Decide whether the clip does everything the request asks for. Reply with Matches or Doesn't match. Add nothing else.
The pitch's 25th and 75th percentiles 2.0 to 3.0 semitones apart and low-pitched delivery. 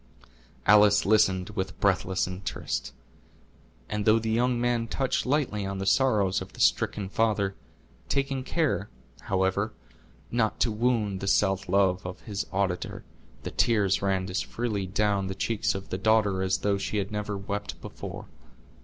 Matches